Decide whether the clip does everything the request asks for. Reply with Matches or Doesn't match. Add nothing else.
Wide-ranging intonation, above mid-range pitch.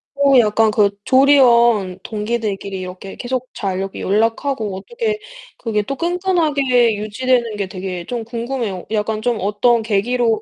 Doesn't match